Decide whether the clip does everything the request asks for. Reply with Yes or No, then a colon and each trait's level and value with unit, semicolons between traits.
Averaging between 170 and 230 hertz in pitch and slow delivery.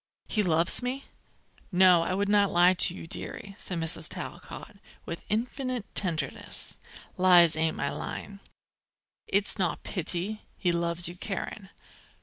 Yes: medium, 185 Hz; slow, 130 wpm